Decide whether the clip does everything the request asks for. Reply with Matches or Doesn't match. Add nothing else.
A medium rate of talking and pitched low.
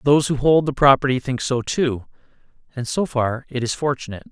Matches